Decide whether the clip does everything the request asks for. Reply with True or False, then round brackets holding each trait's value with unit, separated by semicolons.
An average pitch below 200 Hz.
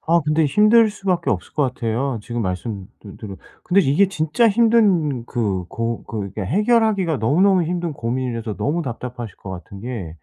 True (135 Hz)